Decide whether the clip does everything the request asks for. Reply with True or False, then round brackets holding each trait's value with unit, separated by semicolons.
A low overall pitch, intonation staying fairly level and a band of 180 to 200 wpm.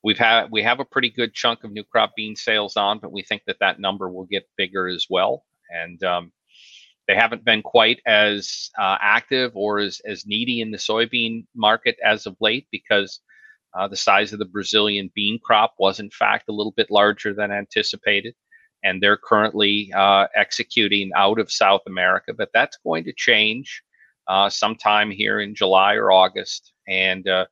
True (105 Hz; 1.9 semitones; 190 wpm)